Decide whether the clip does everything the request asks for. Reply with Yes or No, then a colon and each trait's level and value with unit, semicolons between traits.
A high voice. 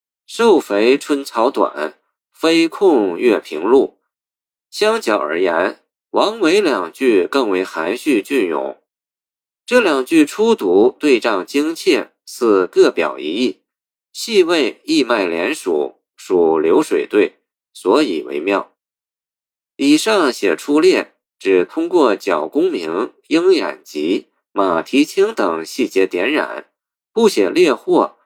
Yes: very high, 370 Hz